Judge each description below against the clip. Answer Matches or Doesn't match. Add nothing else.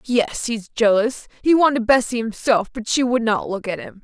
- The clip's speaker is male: Doesn't match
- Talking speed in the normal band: Matches